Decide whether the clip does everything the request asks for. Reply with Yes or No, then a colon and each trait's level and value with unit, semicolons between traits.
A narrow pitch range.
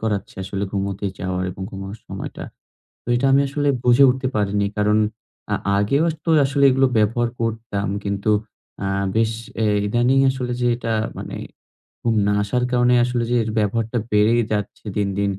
No: average, 3.3 semitones